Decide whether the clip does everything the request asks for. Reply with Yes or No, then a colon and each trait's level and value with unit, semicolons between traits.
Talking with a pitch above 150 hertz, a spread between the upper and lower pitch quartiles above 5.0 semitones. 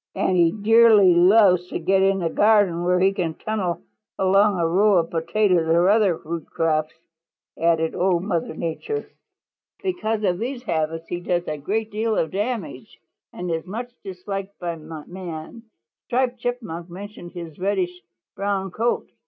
No: medium, 185 Hz; average, 3.8 semitones